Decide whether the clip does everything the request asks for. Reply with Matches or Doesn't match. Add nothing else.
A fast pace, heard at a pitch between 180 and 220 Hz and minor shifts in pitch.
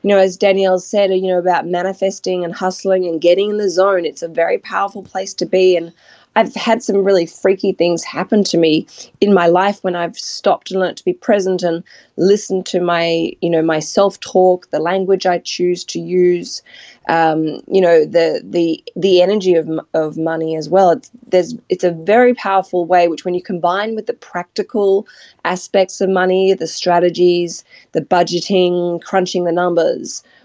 Doesn't match